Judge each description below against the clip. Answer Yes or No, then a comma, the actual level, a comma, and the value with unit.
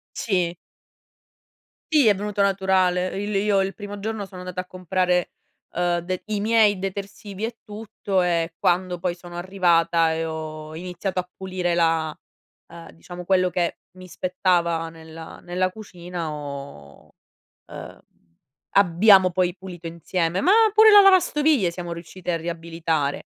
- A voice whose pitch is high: No, medium, 180 Hz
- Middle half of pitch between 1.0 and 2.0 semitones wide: No, narrow, 2.6 semitones